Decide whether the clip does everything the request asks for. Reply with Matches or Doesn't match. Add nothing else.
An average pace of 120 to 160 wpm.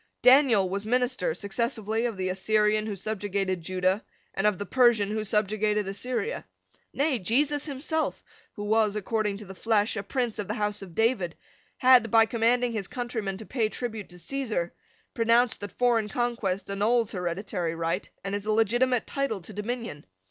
Doesn't match